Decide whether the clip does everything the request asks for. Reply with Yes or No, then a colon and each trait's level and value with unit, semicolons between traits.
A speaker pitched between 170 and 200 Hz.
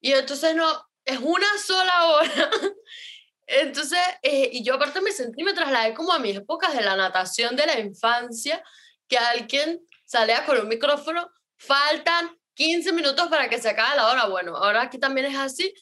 No: very high, 295 Hz